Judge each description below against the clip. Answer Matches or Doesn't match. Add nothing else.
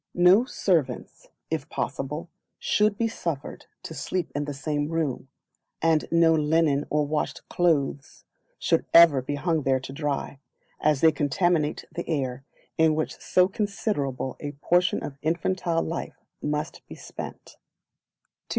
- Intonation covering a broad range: Doesn't match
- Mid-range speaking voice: Matches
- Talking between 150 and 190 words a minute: Doesn't match